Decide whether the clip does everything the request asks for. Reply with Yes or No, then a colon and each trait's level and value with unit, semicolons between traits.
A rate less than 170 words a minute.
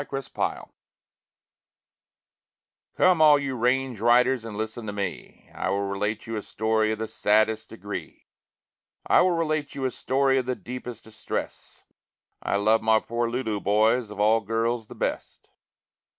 Yes: average, 160 wpm